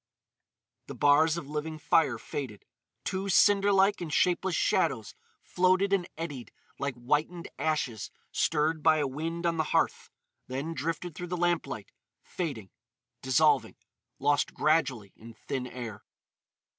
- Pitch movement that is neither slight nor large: Yes, average, 4.5 semitones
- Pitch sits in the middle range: Yes, medium, 155 Hz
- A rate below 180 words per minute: Yes, slow, 135 wpm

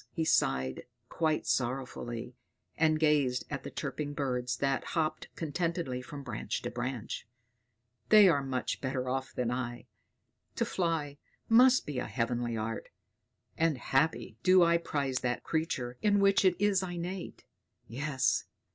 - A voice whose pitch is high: No, medium, 140 Hz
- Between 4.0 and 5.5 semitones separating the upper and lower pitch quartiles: Yes, average, 5.0 semitones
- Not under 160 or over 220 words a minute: No, average, 140 wpm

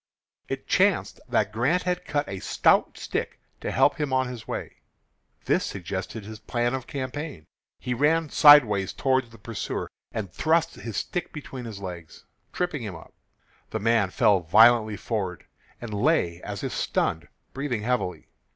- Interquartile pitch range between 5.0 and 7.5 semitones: Yes, wide, 5.5 semitones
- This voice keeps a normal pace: Yes, average, 160 wpm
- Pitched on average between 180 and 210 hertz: No, low, 115 Hz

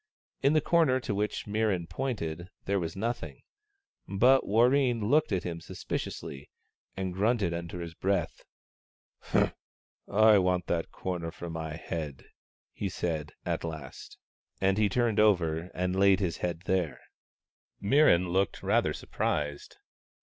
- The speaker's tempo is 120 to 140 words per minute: Yes, slow, 135 wpm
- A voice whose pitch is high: No, very low, 95 Hz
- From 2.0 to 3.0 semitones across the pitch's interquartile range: No, average, 4.4 semitones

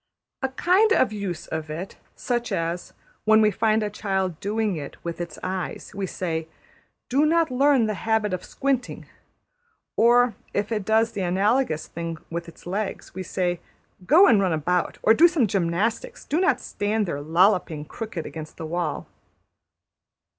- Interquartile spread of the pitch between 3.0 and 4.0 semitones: No, average, 5.2 semitones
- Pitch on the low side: No, high, 200 Hz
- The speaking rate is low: No, average, 165 wpm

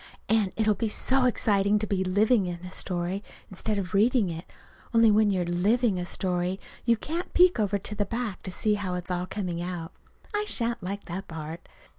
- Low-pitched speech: No, high, 200 Hz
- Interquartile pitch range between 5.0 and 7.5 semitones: No, average, 3.5 semitones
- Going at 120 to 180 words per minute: No, average, 195 wpm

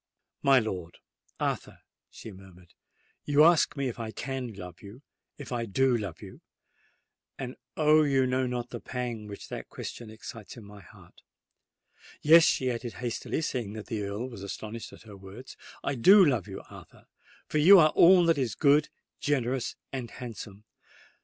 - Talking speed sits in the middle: Yes, average, 155 wpm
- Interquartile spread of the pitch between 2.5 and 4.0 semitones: No, average, 4.6 semitones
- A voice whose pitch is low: Yes, low, 125 Hz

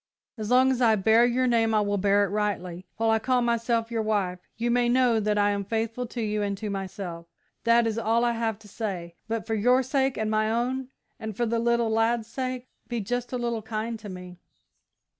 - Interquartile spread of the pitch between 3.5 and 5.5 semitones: No, narrow, 2.4 semitones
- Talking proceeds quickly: Yes, fast, 225 wpm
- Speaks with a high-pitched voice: Yes, high, 225 Hz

